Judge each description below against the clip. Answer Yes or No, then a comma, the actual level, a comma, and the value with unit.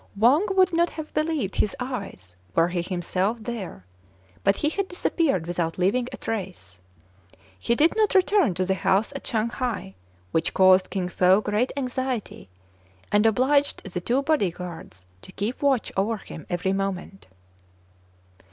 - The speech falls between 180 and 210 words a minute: No, average, 155 wpm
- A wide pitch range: Yes, wide, 6.4 semitones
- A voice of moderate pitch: No, high, 210 Hz